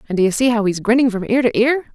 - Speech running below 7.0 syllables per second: No, 7.1 syllables/s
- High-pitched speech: Yes, high, 230 Hz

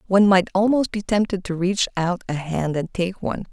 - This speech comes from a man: No, female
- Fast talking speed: Yes, fast, 220 wpm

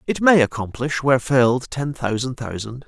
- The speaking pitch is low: Yes, low, 130 Hz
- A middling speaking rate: Yes, average, 165 wpm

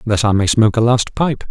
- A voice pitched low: Yes, low, 115 Hz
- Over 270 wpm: Yes, fast, 280 wpm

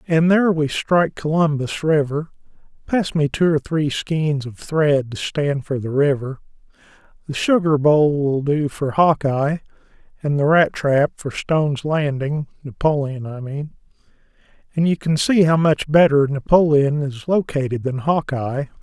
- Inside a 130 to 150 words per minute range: Yes, average, 145 wpm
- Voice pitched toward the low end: No, medium, 150 Hz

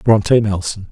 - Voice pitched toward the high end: No, low, 105 Hz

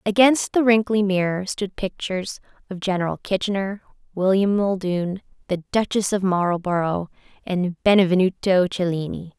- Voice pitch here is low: No, high, 190 Hz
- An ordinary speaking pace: No, slow, 115 wpm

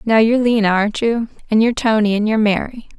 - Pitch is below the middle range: No, high, 220 Hz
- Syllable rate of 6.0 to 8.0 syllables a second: Yes, 6.4 syllables/s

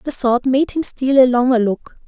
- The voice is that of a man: No, female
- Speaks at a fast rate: Yes, fast, 230 wpm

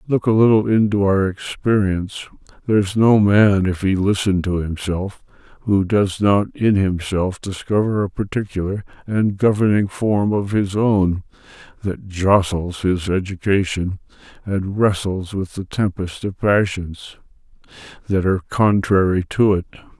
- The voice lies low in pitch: Yes, low, 100 Hz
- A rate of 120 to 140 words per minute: Yes, slow, 135 wpm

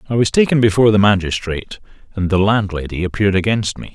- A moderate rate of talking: Yes, average, 185 wpm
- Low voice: Yes, low, 100 Hz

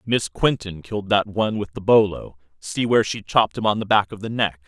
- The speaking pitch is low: Yes, low, 105 Hz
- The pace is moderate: No, fast, 245 wpm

